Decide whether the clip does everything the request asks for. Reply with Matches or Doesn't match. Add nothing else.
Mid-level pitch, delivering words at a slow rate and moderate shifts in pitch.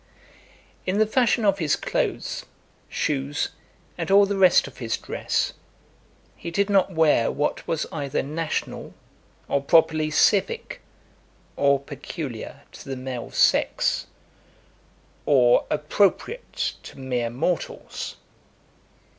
Doesn't match